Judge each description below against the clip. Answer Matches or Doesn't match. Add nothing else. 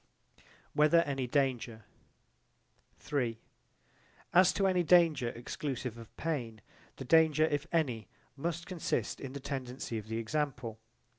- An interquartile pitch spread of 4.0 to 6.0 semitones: Matches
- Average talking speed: Doesn't match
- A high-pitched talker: Doesn't match